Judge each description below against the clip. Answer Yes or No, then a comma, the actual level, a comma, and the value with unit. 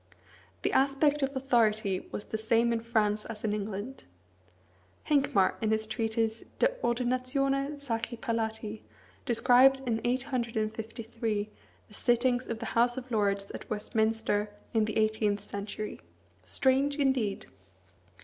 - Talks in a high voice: Yes, high, 230 Hz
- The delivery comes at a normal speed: No, slow, 125 wpm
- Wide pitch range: No, average, 2.9 semitones